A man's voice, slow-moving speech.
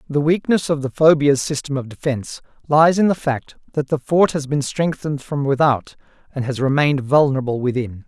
No: male; average, 185 wpm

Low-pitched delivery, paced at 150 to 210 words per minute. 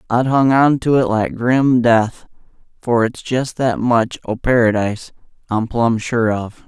Yes: low, 120 Hz; average, 170 wpm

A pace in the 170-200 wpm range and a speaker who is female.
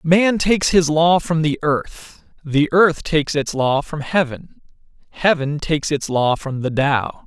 No: average, 175 wpm; male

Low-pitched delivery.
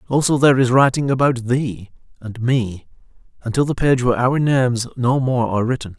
Yes: low, 125 Hz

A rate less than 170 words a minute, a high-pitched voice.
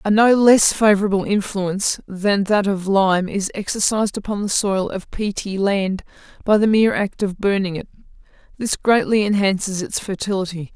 Yes: average, 160 wpm; high, 200 Hz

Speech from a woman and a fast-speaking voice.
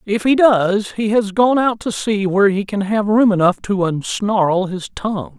No: male; fast, 210 wpm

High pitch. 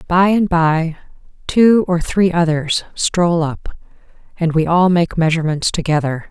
No: medium, 170 Hz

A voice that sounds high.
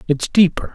No: medium, 165 Hz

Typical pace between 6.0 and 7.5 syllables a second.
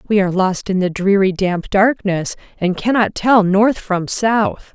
No: 4.1 syllables/s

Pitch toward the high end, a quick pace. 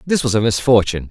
No: low, 110 Hz; fast, 220 wpm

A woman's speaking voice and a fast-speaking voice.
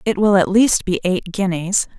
Yes: female; fast, 210 wpm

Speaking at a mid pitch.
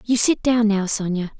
No: high, 215 Hz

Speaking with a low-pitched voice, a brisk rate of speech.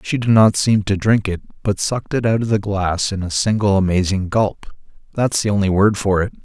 Yes: low, 100 Hz; fast, 225 wpm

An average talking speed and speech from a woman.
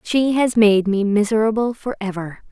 Yes: average, 145 wpm; female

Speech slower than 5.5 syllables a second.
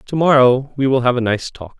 Yes: 5.3 syllables/s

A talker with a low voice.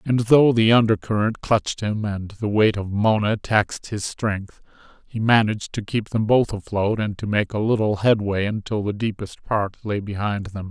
Yes: low, 105 Hz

